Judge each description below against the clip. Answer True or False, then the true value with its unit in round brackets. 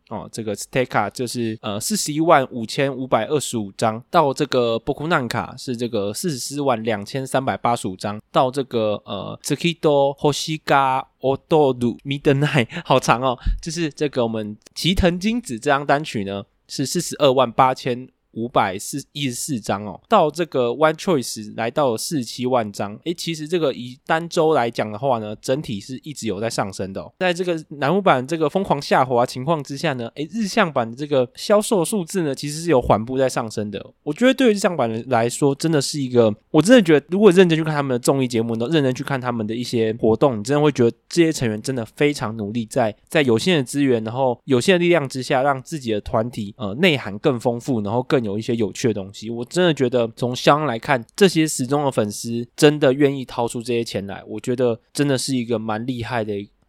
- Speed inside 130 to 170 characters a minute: False (335 characters per minute)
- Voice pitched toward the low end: True (130 Hz)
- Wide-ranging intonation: False (4.7 semitones)